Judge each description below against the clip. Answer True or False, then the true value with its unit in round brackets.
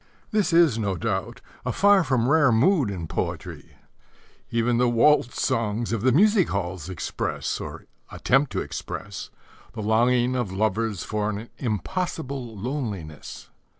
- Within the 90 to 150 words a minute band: True (140 wpm)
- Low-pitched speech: True (115 Hz)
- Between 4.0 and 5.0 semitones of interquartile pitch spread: True (4.6 semitones)